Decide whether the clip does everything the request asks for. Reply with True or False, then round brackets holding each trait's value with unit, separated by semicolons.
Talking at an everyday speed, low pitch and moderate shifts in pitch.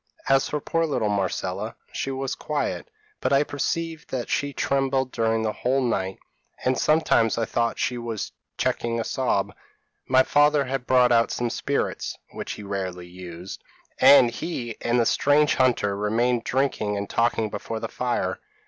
True (165 wpm; 120 Hz; 4.1 semitones)